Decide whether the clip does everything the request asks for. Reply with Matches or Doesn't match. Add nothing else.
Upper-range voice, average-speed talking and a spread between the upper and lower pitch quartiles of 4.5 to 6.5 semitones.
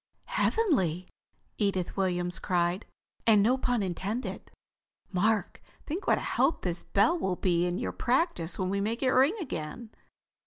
Matches